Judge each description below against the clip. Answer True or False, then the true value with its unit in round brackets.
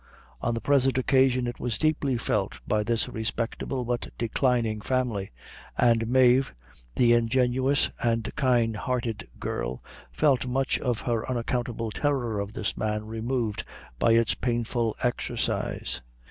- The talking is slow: True (130 wpm)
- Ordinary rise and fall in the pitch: False (2.3 semitones)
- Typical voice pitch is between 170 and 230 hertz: False (120 Hz)